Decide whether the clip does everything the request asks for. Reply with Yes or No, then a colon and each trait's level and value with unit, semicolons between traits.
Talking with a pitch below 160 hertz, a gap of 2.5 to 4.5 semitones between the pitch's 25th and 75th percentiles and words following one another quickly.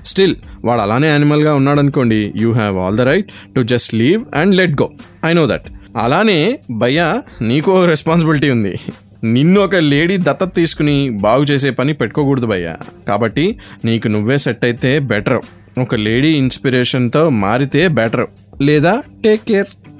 No: medium, 140 Hz; average, 5.1 semitones; fast, 150 wpm